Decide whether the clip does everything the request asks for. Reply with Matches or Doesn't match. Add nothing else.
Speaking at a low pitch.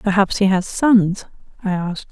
Doesn't match